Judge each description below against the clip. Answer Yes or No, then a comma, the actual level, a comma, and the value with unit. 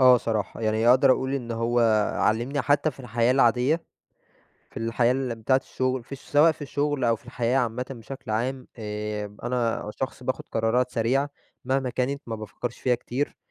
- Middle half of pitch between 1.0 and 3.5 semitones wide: Yes, narrow, 2.6 semitones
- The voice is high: No, low, 125 Hz